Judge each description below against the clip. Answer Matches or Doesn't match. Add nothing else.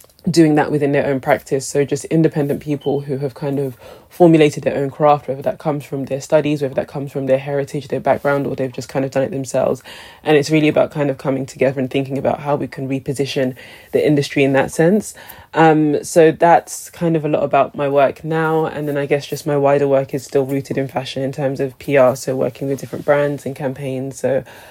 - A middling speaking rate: Doesn't match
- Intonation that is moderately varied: Doesn't match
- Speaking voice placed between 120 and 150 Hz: Matches